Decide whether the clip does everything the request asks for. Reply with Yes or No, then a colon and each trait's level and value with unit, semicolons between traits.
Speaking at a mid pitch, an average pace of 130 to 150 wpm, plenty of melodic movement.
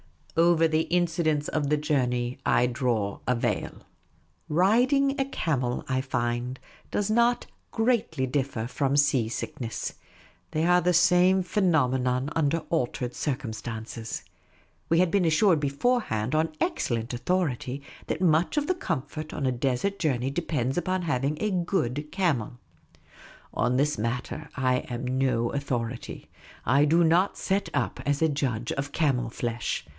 Yes: medium, 145 Hz; average, 145 wpm; wide, 5.7 semitones